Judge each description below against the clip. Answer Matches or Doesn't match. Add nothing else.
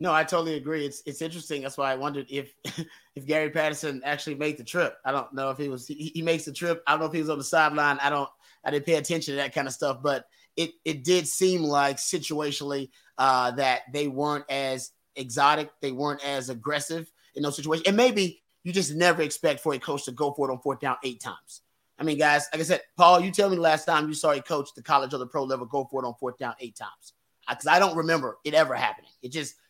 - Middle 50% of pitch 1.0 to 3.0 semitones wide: Matches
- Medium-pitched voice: Matches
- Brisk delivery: Matches